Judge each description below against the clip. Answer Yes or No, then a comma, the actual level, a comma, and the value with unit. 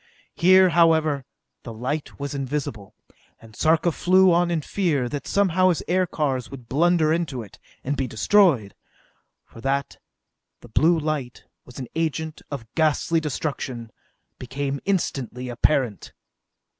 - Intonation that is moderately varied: Yes, average, 4.7 semitones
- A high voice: No, medium, 150 Hz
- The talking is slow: Yes, slow, 130 wpm